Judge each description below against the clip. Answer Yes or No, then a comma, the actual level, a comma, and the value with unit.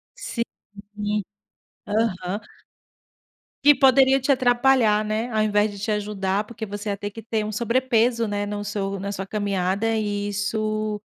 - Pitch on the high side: Yes, high, 210 Hz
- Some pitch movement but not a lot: No, narrow, 2.1 semitones